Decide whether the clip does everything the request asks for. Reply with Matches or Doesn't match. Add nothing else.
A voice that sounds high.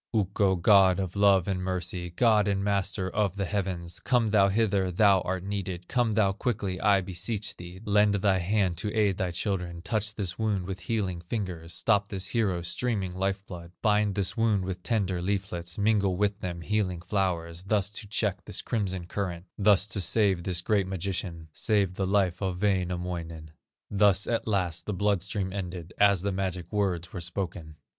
Doesn't match